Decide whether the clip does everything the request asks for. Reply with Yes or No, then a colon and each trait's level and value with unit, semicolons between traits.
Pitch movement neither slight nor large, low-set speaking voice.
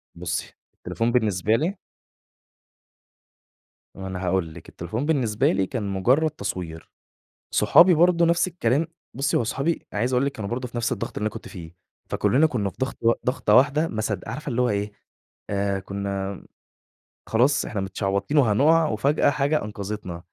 No: wide, 6.1 semitones; low, 115 Hz